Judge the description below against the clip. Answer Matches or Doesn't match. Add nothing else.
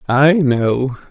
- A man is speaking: Matches